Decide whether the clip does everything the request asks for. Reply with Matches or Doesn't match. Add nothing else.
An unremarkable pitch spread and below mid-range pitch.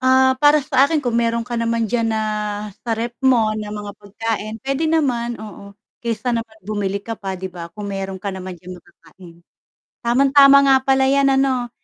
Doesn't match